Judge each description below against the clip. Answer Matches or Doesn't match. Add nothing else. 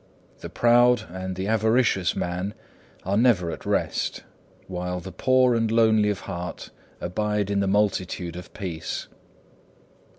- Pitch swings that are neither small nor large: Matches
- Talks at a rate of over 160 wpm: Doesn't match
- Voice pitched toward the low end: Matches